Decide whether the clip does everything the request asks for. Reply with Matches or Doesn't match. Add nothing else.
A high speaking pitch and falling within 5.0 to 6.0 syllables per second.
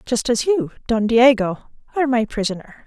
Matches